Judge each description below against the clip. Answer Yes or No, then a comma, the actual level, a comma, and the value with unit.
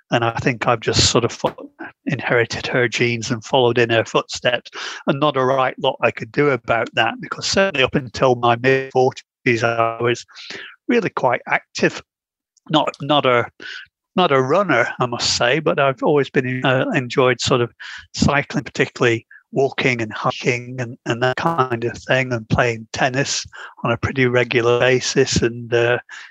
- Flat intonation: Yes, narrow, 2.0 semitones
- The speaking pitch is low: Yes, low, 125 Hz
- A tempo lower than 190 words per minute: Yes, average, 170 wpm